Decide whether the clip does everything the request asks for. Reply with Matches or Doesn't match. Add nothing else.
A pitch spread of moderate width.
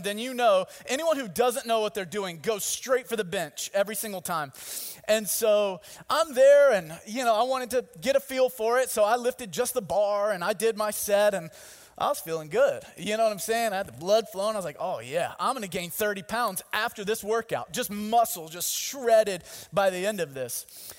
Matches